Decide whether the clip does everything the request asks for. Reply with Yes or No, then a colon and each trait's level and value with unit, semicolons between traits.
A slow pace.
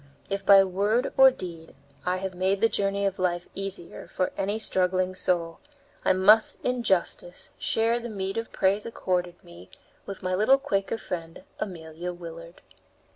No: average, 160 wpm